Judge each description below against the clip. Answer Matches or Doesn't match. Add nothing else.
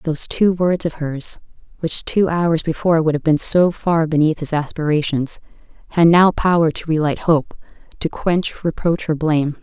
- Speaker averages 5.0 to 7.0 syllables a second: Doesn't match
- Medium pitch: Matches